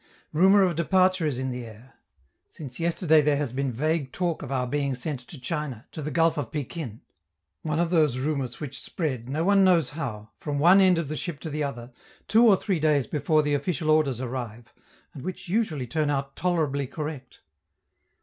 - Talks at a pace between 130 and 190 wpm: No, average, 200 wpm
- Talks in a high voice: No, medium, 150 Hz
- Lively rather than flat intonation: No, average, 4.0 semitones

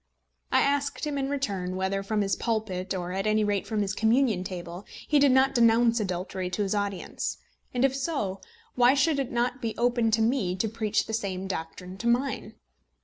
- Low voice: No, high, 220 Hz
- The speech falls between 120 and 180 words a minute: No, average, 200 wpm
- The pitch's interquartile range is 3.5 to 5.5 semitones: Yes, average, 4.7 semitones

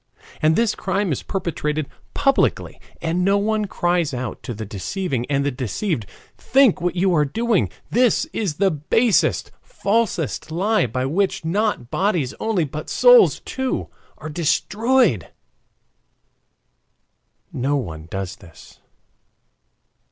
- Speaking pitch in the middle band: Yes, medium, 175 Hz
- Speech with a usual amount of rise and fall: No, wide, 7.2 semitones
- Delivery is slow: Yes, slow, 125 wpm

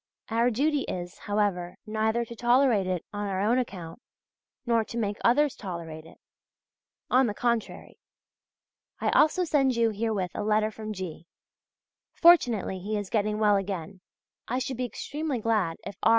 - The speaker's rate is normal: Yes, average, 160 wpm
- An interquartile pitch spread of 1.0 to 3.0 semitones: No, average, 3.7 semitones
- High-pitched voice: Yes, high, 215 Hz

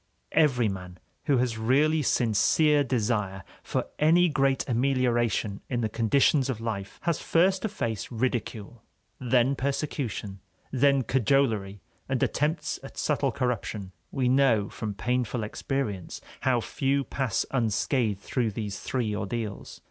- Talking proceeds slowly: Yes, slow, 130 wpm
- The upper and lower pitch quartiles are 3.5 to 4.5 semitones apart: Yes, average, 4.2 semitones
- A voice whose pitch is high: No, low, 125 Hz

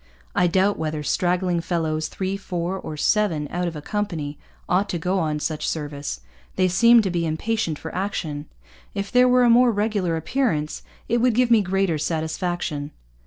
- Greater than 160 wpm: Yes, average, 175 wpm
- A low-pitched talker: No, medium, 180 Hz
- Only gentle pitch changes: No, average, 4.6 semitones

